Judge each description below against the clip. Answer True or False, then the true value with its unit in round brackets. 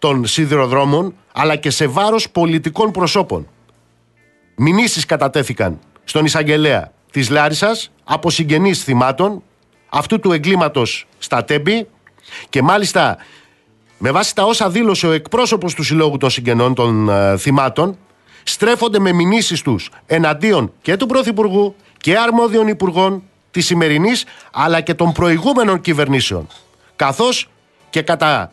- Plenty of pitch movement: True (6.2 semitones)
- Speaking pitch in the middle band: True (165 Hz)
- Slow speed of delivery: False (125 wpm)